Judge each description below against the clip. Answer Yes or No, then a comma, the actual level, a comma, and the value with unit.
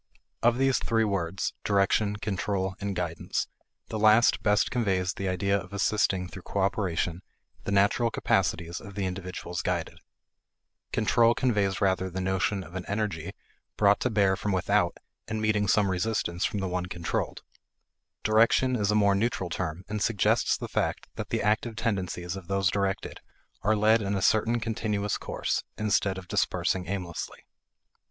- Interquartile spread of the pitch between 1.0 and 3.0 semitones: Yes, narrow, 2.4 semitones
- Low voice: Yes, low, 100 Hz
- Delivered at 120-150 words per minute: No, average, 160 wpm